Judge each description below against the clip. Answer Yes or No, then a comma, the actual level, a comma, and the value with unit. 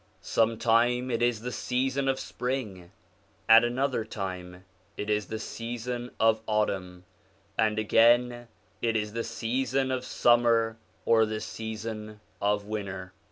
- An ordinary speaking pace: No, slow, 130 wpm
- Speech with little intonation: Yes, narrow, 2.3 semitones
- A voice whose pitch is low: Yes, low, 115 Hz